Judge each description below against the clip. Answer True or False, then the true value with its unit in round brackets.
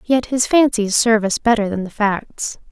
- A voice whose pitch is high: True (225 Hz)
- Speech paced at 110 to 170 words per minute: False (200 wpm)